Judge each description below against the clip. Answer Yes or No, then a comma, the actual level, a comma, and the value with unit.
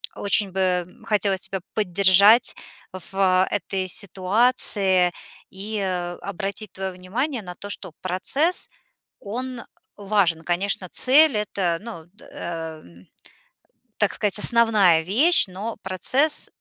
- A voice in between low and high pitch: No, high, 195 Hz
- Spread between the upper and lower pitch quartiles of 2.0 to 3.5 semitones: Yes, average, 3.0 semitones